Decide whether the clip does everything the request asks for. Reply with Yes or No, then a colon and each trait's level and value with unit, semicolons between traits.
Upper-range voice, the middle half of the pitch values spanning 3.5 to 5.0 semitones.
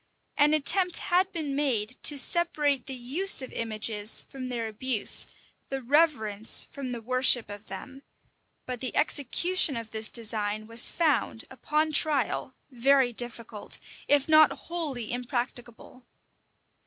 Yes: very high, 255 Hz; average, 4.4 semitones